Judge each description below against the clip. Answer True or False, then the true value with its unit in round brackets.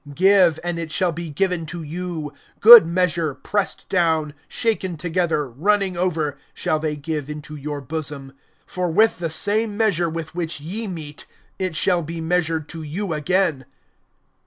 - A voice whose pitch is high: False (165 Hz)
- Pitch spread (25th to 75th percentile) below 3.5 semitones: True (3.1 semitones)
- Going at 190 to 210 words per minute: False (160 wpm)